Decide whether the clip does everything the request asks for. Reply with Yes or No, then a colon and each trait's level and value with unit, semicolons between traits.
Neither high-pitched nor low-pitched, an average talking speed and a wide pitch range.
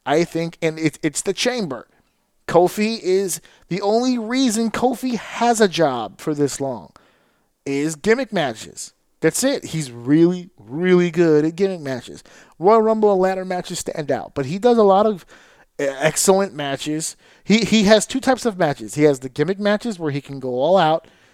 Yes: medium, 175 Hz; average, 180 wpm; wide, 5.7 semitones